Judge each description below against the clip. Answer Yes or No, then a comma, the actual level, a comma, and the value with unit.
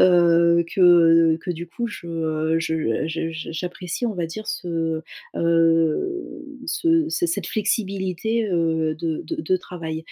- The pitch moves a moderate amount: Yes, average, 3.0 semitones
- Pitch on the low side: No, medium, 170 Hz